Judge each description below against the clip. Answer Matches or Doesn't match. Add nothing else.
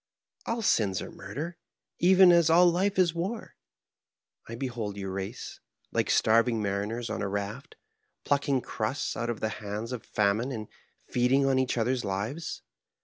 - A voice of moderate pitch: Doesn't match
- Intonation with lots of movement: Matches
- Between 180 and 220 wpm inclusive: Doesn't match